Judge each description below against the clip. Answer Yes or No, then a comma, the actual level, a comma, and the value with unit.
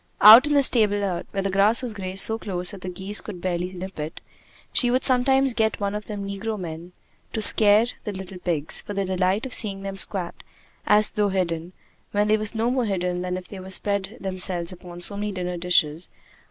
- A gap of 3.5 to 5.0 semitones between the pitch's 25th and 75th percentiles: No, average, 2.8 semitones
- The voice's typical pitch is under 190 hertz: No, high, 195 Hz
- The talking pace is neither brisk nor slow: No, fast, 220 wpm